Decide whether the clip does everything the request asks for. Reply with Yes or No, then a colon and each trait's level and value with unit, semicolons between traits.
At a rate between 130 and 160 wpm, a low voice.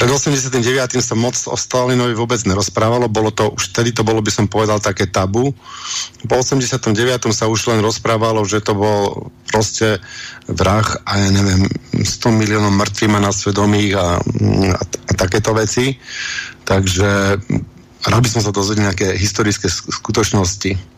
Yes: average, 150 wpm; low, 110 Hz